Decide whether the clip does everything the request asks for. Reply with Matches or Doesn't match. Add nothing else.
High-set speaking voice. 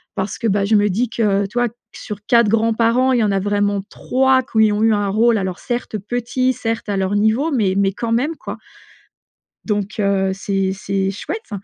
Matches